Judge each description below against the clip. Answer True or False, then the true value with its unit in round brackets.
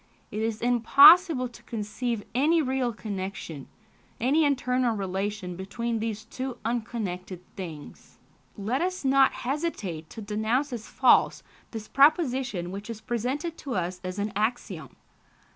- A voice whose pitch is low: False (230 Hz)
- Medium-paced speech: False (130 wpm)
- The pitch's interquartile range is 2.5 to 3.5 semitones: False (4.5 semitones)